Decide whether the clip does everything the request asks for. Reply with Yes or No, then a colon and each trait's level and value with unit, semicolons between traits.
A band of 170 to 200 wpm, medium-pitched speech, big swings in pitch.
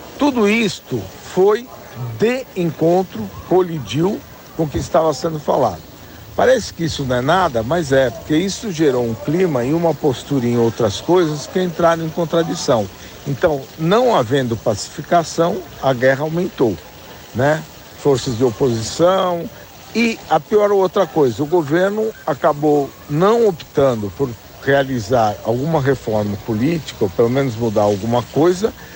No: average, 140 wpm; medium, 155 Hz; wide, 5.8 semitones